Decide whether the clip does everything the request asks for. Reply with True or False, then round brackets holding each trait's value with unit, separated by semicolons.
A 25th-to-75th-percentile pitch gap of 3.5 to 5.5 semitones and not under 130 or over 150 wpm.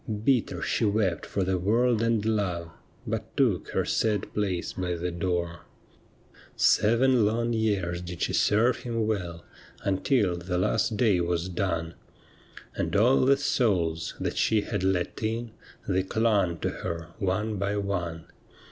True (4.1 semitones; 145 wpm)